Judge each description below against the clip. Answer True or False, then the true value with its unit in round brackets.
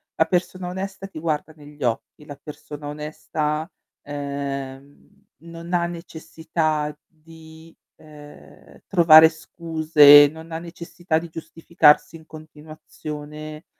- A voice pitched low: False (155 Hz)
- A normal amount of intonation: False (1.9 semitones)